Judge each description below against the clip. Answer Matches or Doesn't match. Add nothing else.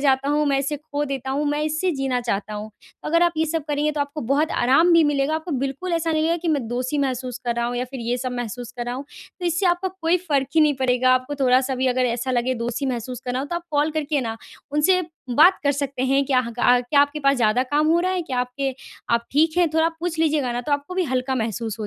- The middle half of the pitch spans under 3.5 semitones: Doesn't match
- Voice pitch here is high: Matches